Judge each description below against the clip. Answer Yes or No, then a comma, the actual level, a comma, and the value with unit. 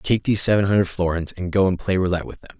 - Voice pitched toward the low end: Yes, very low, 95 Hz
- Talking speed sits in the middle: No, fast, 275 wpm